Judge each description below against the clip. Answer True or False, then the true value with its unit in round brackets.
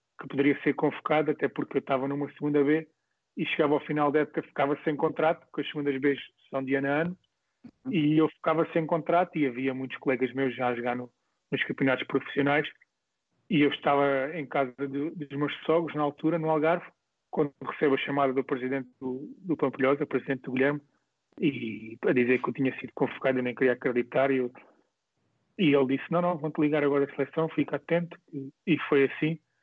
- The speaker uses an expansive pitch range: False (2.4 semitones)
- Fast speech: True (200 wpm)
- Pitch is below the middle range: False (145 Hz)